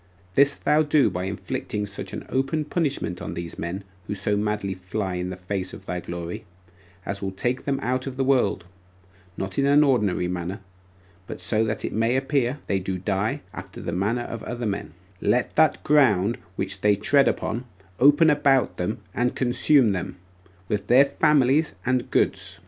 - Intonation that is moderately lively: No, wide, 5.9 semitones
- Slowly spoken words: No, average, 175 wpm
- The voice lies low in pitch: Yes, low, 110 Hz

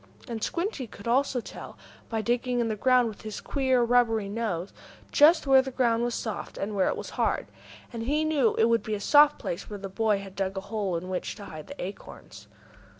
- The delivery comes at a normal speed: No, fast, 225 wpm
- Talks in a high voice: Yes, high, 225 Hz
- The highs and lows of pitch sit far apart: No, average, 4.1 semitones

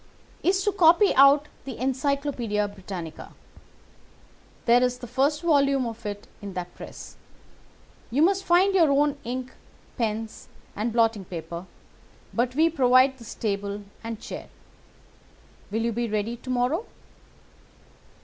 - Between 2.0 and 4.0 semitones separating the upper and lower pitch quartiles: No, average, 4.9 semitones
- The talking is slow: Yes, slow, 130 wpm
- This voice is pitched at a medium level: No, high, 245 Hz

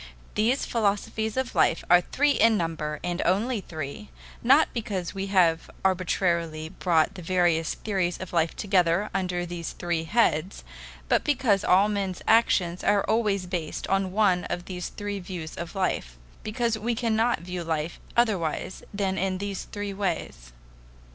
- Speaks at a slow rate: No, average, 155 wpm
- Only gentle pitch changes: No, average, 3.4 semitones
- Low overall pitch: No, medium, 185 Hz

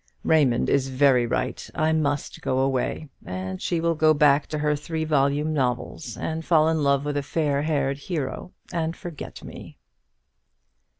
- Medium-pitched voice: Yes, medium, 145 Hz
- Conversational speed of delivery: Yes, average, 165 wpm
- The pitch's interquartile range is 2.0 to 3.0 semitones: Yes, average, 2.7 semitones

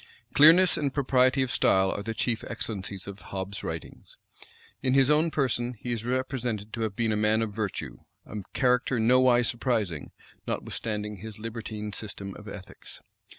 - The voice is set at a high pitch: No, low, 115 Hz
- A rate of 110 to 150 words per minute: No, average, 160 wpm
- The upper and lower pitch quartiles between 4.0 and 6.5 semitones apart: No, average, 3.4 semitones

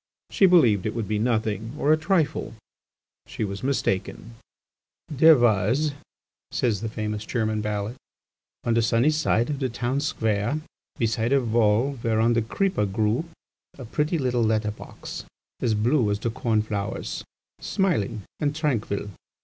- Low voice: Yes, low, 115 Hz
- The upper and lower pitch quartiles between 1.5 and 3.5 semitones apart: No, average, 4.6 semitones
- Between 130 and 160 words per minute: Yes, average, 150 wpm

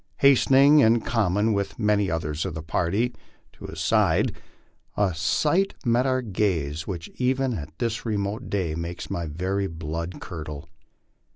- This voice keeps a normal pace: Yes, average, 150 wpm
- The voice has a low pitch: Yes, low, 100 Hz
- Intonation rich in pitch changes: Yes, wide, 6.1 semitones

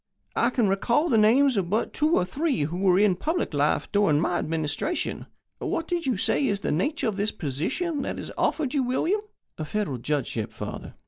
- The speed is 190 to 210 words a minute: Yes, average, 200 wpm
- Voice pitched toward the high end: Yes, high, 210 Hz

